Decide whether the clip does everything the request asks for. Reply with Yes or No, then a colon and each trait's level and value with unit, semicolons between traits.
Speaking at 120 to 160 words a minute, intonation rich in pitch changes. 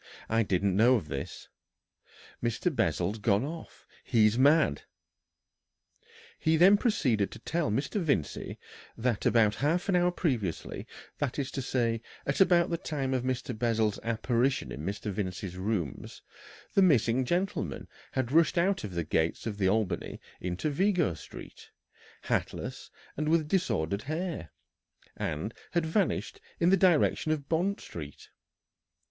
Yes: average, 140 wpm; wide, 8.1 semitones